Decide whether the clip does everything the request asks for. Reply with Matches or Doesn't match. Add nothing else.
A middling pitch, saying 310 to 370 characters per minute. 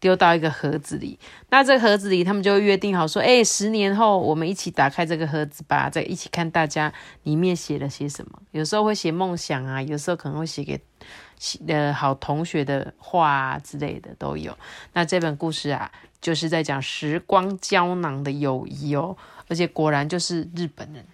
Doesn't match